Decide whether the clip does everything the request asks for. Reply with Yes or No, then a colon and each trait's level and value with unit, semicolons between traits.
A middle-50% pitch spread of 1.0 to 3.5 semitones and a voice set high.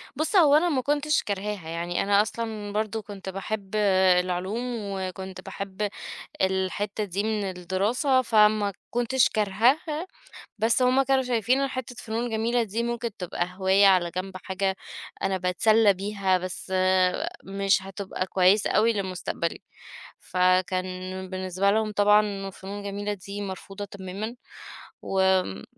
Yes: average, 2.9 semitones; high, 200 Hz